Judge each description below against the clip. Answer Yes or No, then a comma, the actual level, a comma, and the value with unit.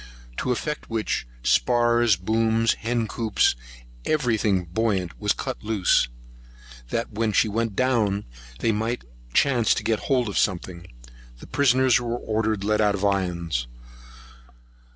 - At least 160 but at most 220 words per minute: No, average, 150 wpm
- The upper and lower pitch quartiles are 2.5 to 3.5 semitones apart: Yes, average, 3.1 semitones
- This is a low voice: Yes, low, 110 Hz